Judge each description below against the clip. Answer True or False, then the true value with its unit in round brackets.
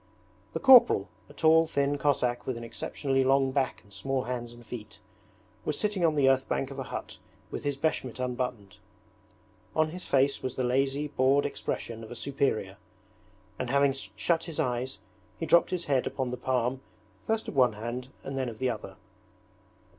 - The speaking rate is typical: True (185 wpm)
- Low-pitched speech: True (130 Hz)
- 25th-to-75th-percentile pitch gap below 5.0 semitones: True (2.6 semitones)